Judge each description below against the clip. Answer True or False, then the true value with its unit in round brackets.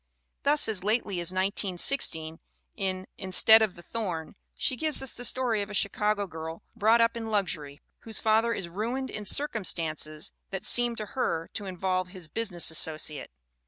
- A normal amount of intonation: True (4.7 semitones)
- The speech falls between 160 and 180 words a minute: True (165 wpm)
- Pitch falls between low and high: False (200 Hz)